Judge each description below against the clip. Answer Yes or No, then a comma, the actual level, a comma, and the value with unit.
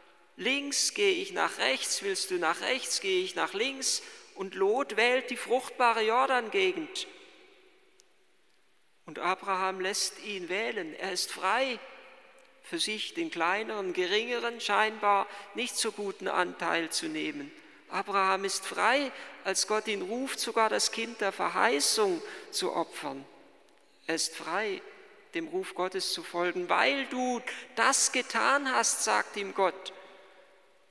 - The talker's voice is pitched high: Yes, very high, 255 Hz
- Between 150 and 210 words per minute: No, average, 135 wpm